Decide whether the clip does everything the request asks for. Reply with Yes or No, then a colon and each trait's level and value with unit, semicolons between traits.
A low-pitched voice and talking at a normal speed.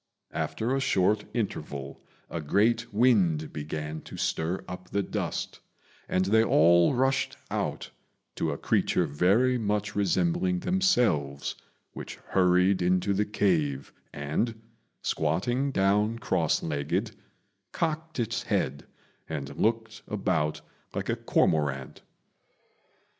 No: very low, 95 Hz; slow, 115 wpm